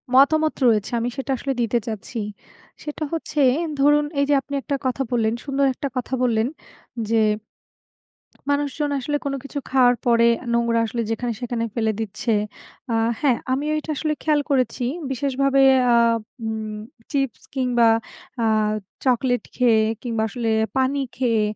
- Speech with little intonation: No, average, 3.3 semitones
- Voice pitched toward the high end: Yes, very high, 250 Hz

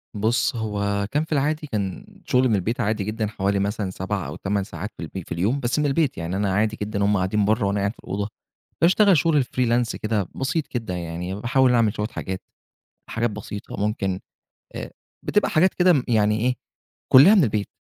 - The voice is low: Yes, low, 105 Hz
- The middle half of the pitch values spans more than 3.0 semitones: Yes, average, 4.1 semitones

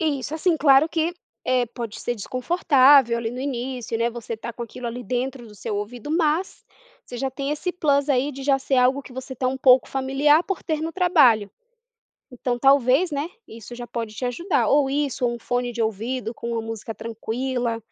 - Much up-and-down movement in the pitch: No, average, 3.3 semitones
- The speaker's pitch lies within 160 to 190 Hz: No, very high, 255 Hz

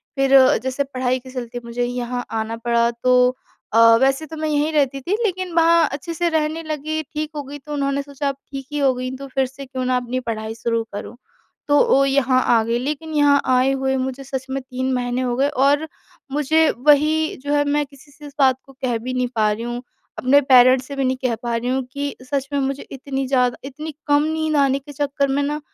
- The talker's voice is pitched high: Yes, very high, 270 Hz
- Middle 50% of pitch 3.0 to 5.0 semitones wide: No, narrow, 2.4 semitones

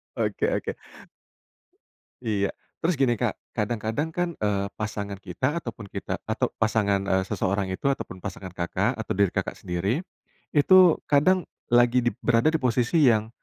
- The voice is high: No, low, 110 Hz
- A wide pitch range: Yes, wide, 5.7 semitones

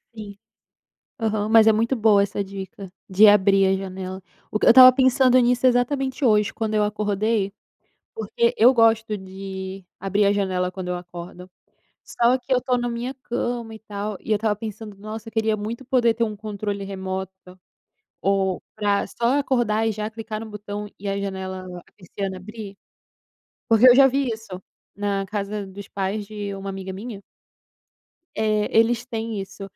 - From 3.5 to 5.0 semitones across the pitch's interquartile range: No, narrow, 2.6 semitones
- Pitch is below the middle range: No, high, 210 Hz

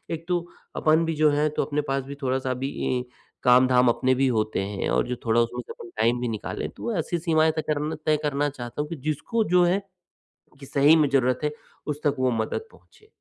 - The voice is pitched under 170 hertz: Yes, medium, 140 Hz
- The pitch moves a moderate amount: Yes, average, 3.8 semitones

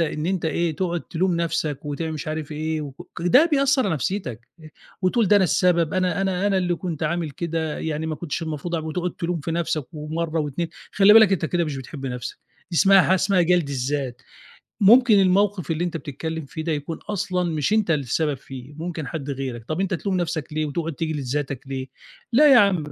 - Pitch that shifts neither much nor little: Yes, average, 3.5 semitones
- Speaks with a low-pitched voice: No, medium, 165 Hz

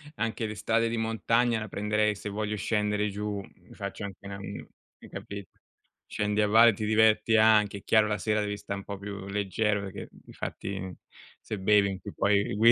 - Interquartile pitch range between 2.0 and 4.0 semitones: No, narrow, 1.5 semitones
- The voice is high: No, low, 105 Hz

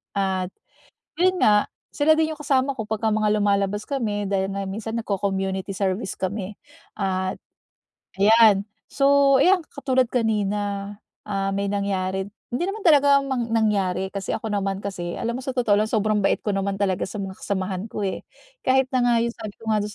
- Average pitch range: Yes, average, 3.8 semitones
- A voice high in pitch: Yes, high, 210 Hz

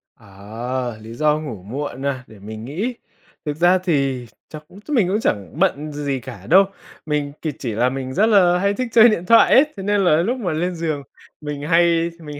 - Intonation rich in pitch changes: Yes, wide, 6.0 semitones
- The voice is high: No, medium, 150 Hz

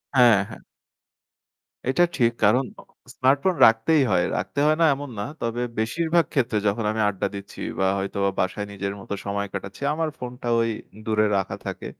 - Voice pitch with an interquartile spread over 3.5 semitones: Yes, average, 5.3 semitones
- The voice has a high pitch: No, low, 115 Hz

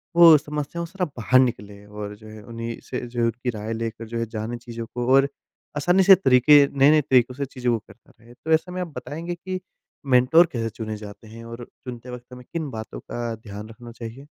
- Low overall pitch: Yes, low, 120 Hz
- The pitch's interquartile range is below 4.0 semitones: No, average, 4.3 semitones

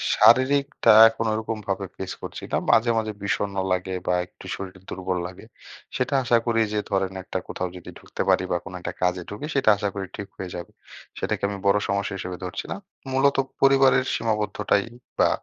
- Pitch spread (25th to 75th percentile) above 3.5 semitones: Yes, average, 4.0 semitones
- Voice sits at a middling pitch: No, low, 100 Hz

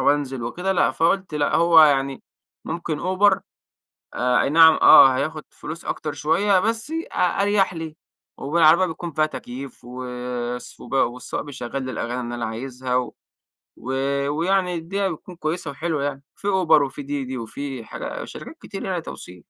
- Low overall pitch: No, medium, 150 Hz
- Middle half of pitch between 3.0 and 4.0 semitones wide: No, average, 4.8 semitones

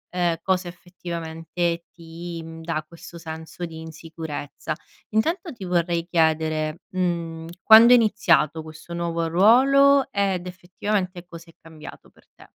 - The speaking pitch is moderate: Yes, medium, 170 Hz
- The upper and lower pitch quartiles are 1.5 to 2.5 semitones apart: Yes, narrow, 2.2 semitones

